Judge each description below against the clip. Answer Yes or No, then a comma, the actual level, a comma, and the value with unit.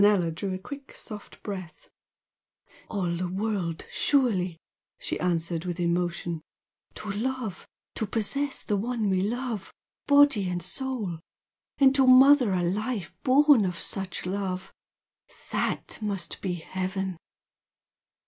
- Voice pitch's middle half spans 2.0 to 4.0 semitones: No, average, 5.2 semitones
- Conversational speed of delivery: No, slow, 125 wpm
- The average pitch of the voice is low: No, high, 195 Hz